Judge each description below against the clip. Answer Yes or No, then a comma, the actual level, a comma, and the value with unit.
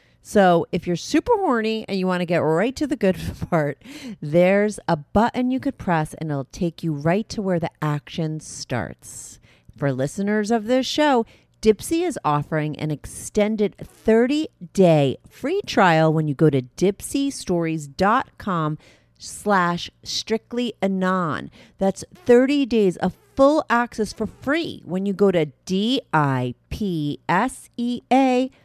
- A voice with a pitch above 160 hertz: Yes, high, 190 Hz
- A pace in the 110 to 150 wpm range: Yes, average, 145 wpm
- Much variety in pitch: Yes, wide, 7.0 semitones